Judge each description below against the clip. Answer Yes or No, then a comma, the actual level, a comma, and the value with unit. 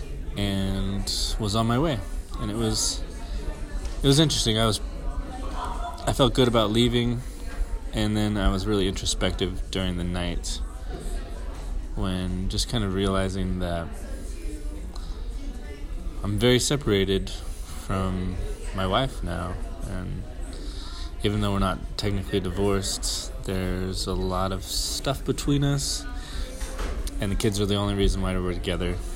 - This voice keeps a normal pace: No, slow, 130 wpm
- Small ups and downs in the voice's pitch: No, average, 4.4 semitones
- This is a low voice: Yes, very low, 95 Hz